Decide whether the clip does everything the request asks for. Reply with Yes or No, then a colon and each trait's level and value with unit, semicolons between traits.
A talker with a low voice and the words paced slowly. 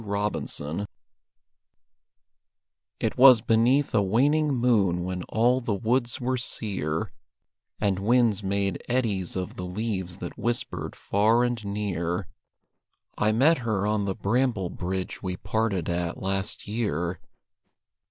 Yes: low, 105 Hz; slow, 125 wpm